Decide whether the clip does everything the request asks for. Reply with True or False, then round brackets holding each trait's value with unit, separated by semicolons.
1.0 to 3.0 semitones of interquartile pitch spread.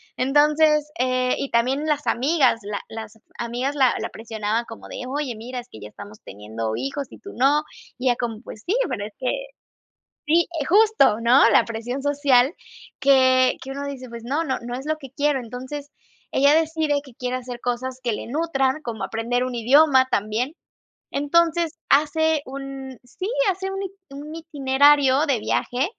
False (3.6 semitones)